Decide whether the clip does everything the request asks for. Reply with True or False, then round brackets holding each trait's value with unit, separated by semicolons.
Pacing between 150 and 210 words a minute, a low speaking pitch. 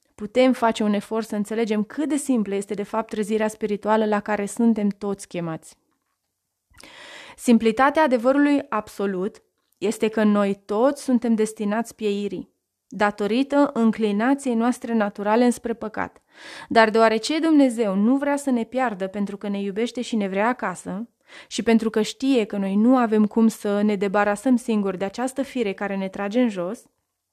False (160 wpm; 220 Hz)